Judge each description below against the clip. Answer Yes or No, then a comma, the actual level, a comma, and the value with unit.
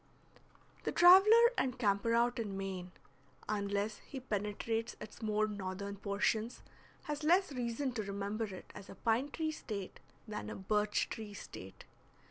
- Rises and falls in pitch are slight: No, average, 3.7 semitones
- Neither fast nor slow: Yes, average, 145 wpm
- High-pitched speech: Yes, high, 215 Hz